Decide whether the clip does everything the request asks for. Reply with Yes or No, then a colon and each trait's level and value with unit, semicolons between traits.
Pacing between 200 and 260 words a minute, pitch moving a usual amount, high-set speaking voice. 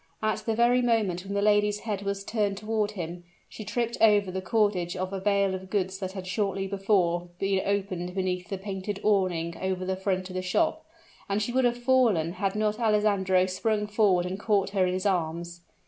No: fast, 205 wpm; narrow, 2.3 semitones; high, 195 Hz